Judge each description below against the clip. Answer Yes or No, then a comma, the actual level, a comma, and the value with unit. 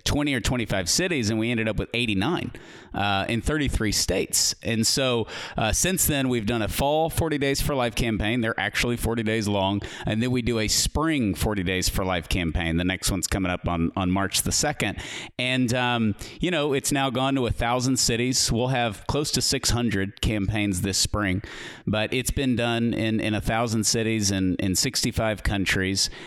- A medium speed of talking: Yes, average, 195 wpm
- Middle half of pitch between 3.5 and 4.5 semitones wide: Yes, average, 4.1 semitones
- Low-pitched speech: Yes, low, 115 Hz